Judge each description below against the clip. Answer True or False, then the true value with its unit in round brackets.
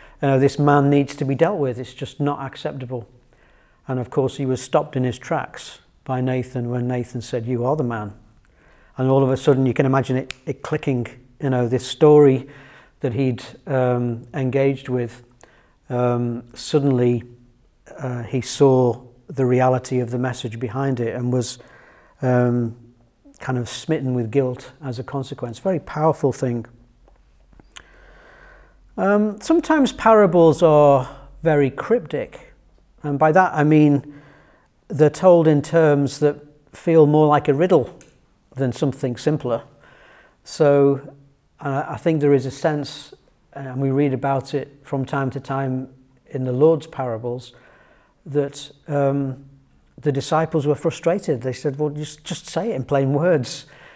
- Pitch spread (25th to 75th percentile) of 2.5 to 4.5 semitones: True (2.9 semitones)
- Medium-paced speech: True (155 wpm)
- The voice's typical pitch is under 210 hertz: True (135 Hz)